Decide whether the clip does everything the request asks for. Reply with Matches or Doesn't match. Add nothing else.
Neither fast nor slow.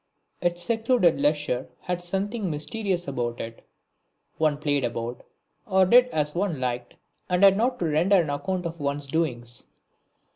Matches